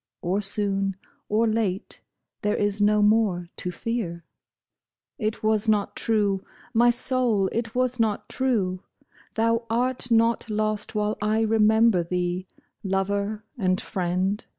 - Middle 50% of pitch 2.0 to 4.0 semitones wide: Yes, average, 2.7 semitones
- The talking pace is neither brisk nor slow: No, slow, 130 wpm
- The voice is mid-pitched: No, high, 210 Hz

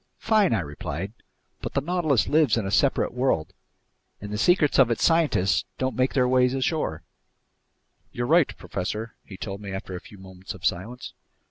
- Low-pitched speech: Yes, low, 115 Hz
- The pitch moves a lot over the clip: Yes, wide, 6.4 semitones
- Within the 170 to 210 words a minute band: Yes, average, 175 wpm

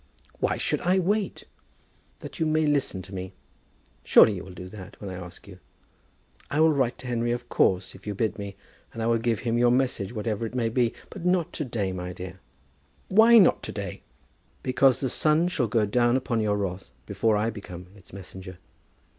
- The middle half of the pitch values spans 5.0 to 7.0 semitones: Yes, average, 5.3 semitones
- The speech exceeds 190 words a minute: Yes, fast, 205 wpm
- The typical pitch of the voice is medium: No, low, 115 Hz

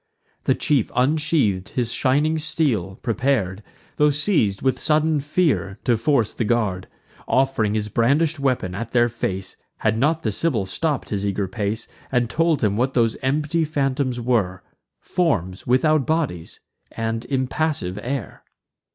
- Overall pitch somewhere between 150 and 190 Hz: No, low, 125 Hz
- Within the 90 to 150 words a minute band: Yes, average, 140 wpm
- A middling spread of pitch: No, wide, 5.9 semitones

